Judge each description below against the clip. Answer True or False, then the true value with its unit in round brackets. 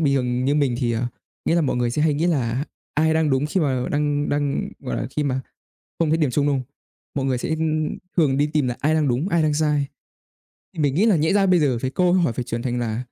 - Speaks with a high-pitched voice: False (145 Hz)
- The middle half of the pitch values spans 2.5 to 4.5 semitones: True (3.5 semitones)